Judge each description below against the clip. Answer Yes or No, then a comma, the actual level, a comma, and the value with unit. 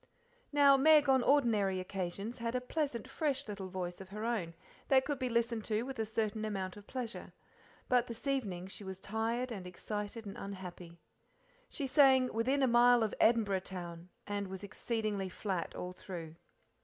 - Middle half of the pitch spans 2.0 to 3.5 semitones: No, average, 4.8 semitones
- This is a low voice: No, high, 220 Hz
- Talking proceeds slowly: No, average, 175 wpm